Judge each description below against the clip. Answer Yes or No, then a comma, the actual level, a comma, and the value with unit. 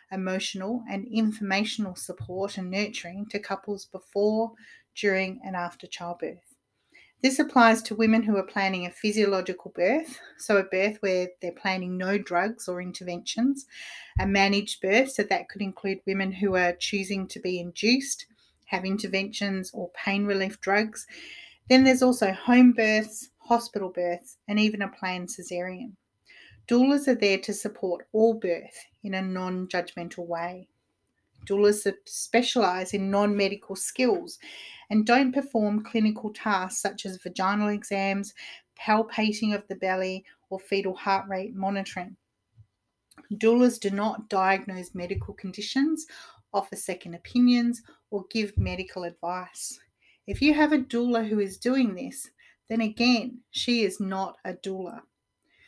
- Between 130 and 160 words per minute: Yes, average, 140 wpm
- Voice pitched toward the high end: Yes, high, 200 Hz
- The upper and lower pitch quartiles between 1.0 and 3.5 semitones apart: Yes, average, 3.0 semitones